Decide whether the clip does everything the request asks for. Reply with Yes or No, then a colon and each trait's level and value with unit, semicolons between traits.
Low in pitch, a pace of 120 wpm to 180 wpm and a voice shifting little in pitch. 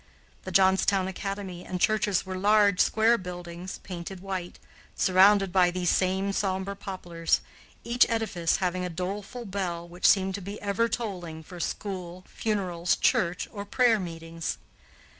No: high, 190 Hz; average, 140 wpm; narrow, 2.3 semitones